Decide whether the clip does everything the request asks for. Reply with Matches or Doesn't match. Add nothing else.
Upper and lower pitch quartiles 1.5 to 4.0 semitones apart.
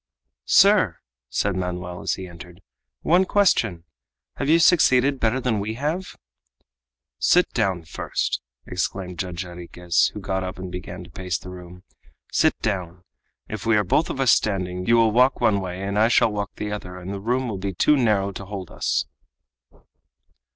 Doesn't match